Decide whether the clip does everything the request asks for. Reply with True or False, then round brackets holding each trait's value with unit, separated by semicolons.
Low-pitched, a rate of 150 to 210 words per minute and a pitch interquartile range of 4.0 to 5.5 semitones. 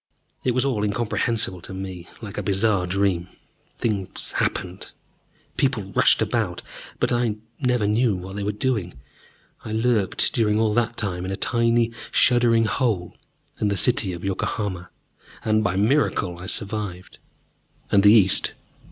False (105 Hz; 155 wpm; 3.5 semitones)